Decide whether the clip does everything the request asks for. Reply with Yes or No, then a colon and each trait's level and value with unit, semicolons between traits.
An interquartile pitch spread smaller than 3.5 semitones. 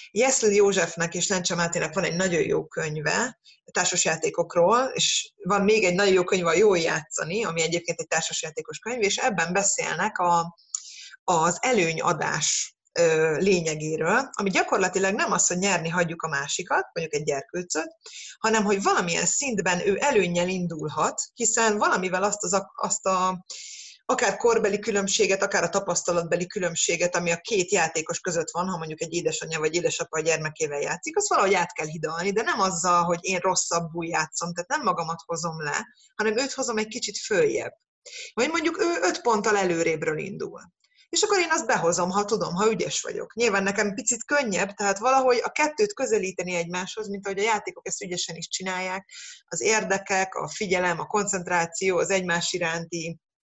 No: average, 4.6 semitones